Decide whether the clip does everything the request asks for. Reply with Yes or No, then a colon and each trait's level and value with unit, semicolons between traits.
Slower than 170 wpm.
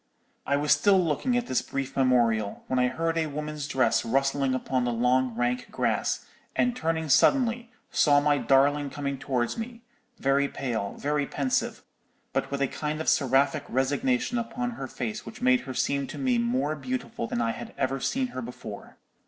No: average, 185 wpm